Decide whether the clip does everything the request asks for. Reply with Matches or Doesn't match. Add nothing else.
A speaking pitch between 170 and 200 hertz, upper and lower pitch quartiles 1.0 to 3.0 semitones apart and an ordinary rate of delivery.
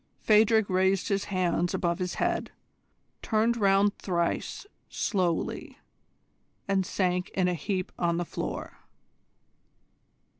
Doesn't match